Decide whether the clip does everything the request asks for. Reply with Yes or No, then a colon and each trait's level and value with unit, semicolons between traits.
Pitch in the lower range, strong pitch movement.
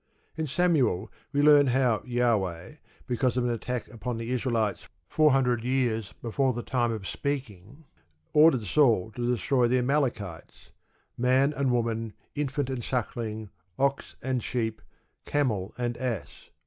No: low, 125 Hz; average, 3.1 semitones